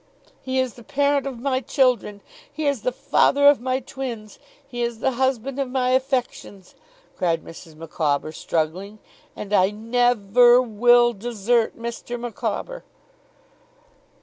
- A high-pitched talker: Yes, high, 240 Hz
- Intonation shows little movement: No, average, 3.9 semitones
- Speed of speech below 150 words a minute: Yes, average, 140 wpm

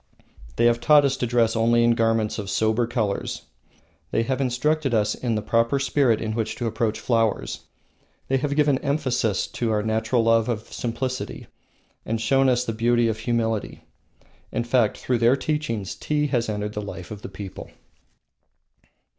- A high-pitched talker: No, low, 115 Hz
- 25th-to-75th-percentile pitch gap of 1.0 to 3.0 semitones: Yes, average, 2.7 semitones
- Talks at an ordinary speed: Yes, average, 170 wpm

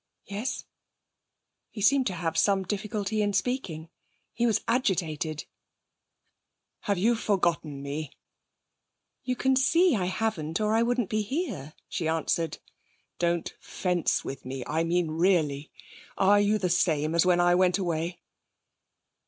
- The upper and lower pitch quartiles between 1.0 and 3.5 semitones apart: No, average, 4.8 semitones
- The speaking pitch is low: No, medium, 180 Hz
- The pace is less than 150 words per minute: Yes, slow, 135 wpm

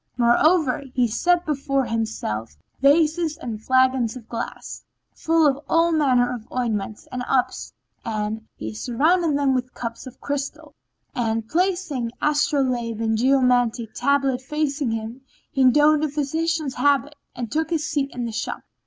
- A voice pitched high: Yes, very high, 260 Hz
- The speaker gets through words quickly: No, average, 145 wpm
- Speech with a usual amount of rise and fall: Yes, average, 4.3 semitones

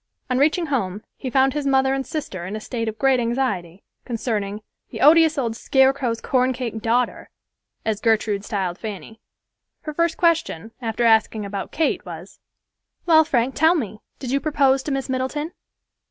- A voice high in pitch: Yes, very high, 250 Hz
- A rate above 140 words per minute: Yes, average, 165 wpm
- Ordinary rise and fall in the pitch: Yes, average, 4.0 semitones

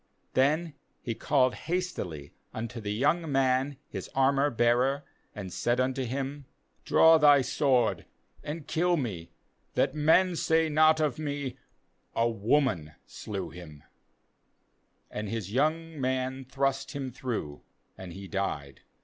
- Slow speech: Yes, slow, 130 wpm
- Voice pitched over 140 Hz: No, low, 130 Hz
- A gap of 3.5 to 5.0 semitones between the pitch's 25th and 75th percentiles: Yes, average, 4.7 semitones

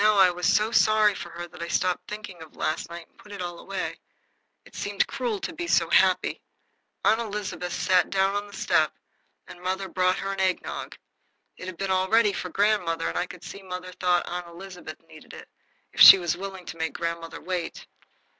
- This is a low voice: No, medium, 185 Hz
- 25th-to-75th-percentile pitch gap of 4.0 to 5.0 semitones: No, narrow, 2.6 semitones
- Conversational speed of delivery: No, fast, 210 wpm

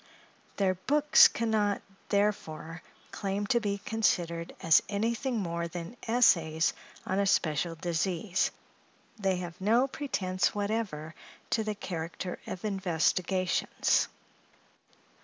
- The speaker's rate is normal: No, slow, 110 wpm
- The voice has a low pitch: No, high, 190 Hz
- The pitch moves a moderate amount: Yes, average, 3.9 semitones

